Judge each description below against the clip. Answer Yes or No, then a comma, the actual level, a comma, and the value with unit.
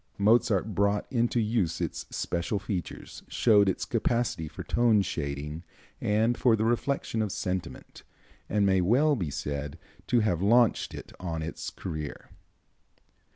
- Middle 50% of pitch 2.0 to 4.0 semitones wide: No, average, 5.2 semitones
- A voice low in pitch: Yes, low, 100 Hz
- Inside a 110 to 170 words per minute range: Yes, average, 140 wpm